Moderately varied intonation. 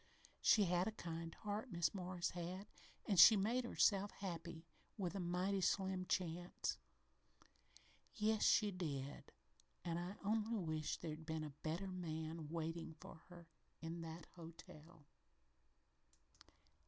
Yes: average, 3.1 semitones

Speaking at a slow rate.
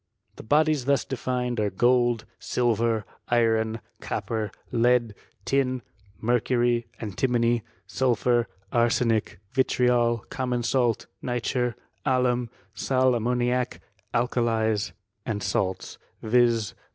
Yes: slow, 95 wpm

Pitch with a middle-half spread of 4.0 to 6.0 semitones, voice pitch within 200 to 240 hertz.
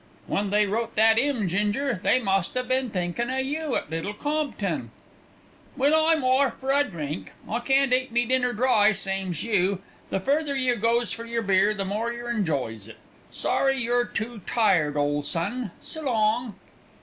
Yes: average, 4.9 semitones; high, 230 Hz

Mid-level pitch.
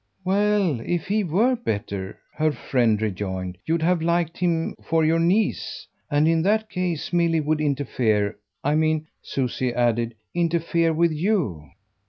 Yes: medium, 160 Hz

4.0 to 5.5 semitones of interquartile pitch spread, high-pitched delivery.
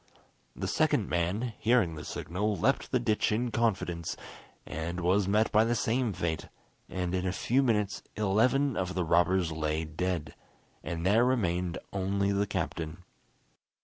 No: average, 4.4 semitones; very low, 95 Hz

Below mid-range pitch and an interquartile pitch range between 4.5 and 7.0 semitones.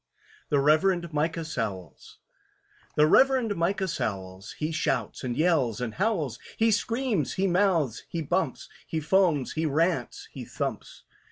No: medium, 160 Hz; wide, 5.5 semitones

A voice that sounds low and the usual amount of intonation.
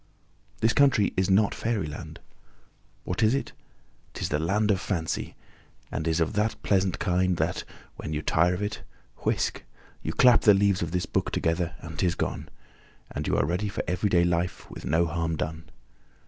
Yes: very low, 90 Hz; average, 3.8 semitones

